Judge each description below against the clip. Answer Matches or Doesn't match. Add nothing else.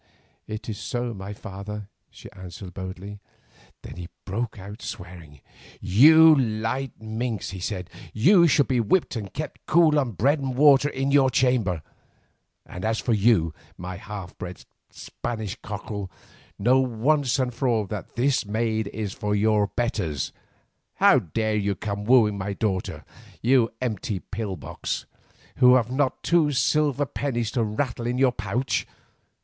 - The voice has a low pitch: Matches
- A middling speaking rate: Matches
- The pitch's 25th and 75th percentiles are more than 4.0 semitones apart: Matches